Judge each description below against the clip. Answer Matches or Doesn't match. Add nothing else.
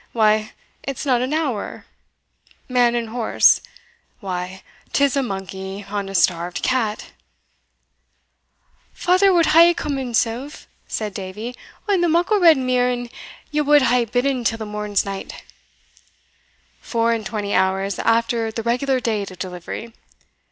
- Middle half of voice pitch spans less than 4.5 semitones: Doesn't match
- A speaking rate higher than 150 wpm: Doesn't match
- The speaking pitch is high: Matches